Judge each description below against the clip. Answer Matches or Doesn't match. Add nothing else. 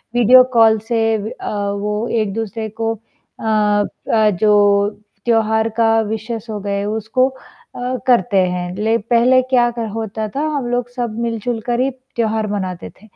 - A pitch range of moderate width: Doesn't match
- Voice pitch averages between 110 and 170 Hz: Doesn't match